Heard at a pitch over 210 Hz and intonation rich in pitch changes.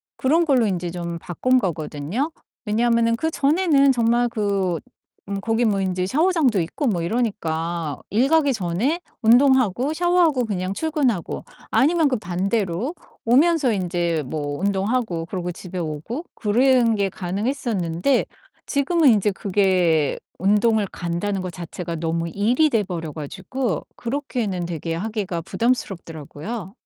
No: high, 205 Hz; wide, 6.5 semitones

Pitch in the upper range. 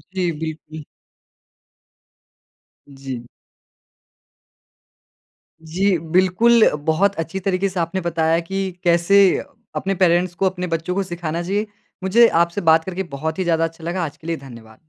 No: medium, 175 Hz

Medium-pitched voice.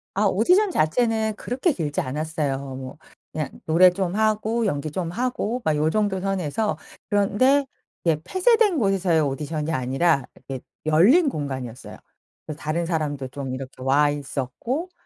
Yes: medium, 165 Hz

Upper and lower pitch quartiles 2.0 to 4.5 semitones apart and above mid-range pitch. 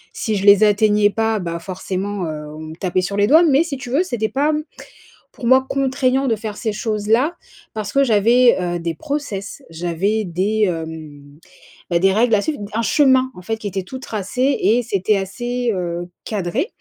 No: wide, 5.4 semitones; high, 210 Hz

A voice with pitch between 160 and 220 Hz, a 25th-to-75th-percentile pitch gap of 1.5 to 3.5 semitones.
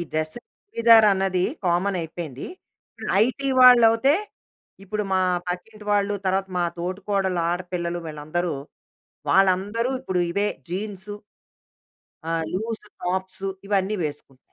Yes: high, 190 Hz; average, 3.2 semitones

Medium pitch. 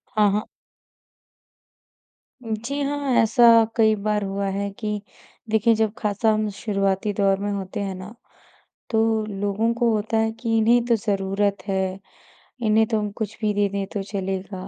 No: high, 210 Hz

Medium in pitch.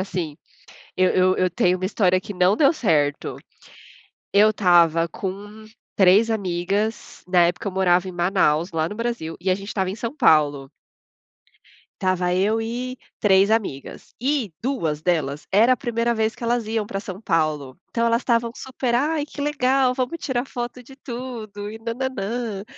No: high, 205 Hz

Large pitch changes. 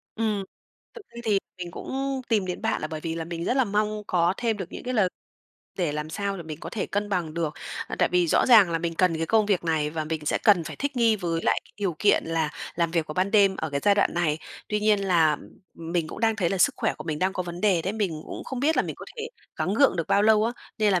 No: average, 4.4 semitones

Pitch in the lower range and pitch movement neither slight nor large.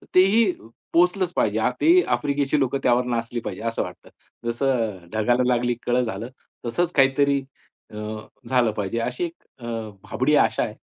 Yes: low, 125 Hz; average, 3.7 semitones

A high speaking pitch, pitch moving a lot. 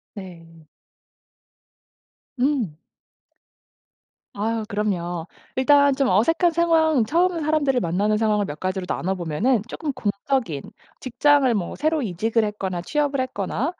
Yes: high, 225 Hz; wide, 7.2 semitones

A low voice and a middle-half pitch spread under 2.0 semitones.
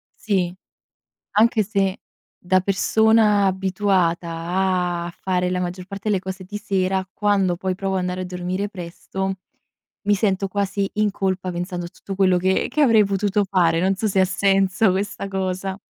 No: high, 190 Hz; narrow, 1.6 semitones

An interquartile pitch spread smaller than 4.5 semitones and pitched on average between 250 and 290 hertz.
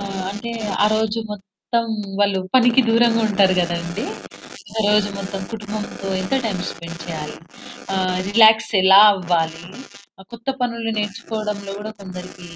No: average, 2.8 semitones; high, 205 Hz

